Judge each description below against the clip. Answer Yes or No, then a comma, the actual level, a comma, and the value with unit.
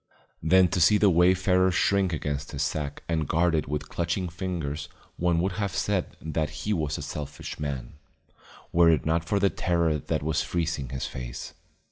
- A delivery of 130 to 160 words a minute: No, average, 180 wpm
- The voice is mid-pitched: No, very low, 80 Hz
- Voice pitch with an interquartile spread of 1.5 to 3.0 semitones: No, average, 3.5 semitones